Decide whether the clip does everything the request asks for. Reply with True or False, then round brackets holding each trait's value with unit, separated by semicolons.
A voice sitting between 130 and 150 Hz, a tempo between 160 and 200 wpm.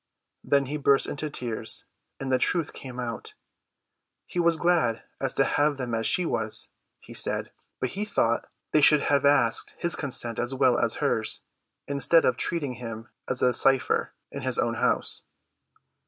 True (135 Hz; 170 wpm)